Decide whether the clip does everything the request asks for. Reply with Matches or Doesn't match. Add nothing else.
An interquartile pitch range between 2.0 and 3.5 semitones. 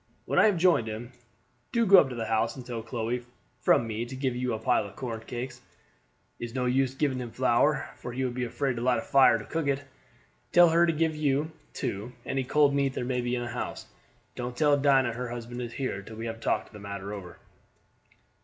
Matches